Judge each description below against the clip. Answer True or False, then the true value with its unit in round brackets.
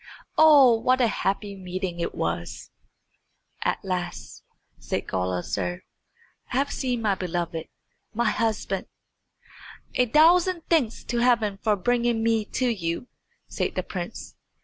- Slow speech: True (125 wpm)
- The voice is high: True (220 Hz)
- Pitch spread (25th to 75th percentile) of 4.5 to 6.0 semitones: True (5.5 semitones)